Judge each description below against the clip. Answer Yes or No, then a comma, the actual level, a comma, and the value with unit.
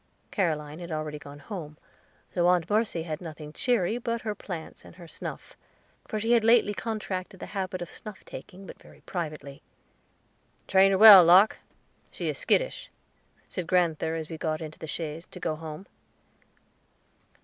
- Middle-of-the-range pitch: Yes, medium, 175 Hz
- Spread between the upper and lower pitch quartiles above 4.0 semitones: Yes, average, 4.5 semitones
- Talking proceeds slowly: No, average, 165 wpm